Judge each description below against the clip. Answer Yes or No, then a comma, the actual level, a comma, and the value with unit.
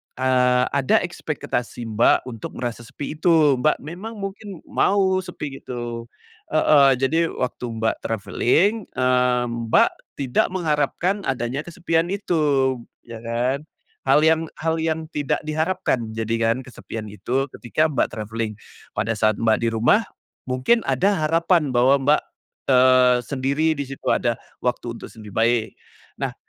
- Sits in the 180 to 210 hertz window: No, low, 130 Hz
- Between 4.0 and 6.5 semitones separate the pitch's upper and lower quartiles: Yes, average, 5.0 semitones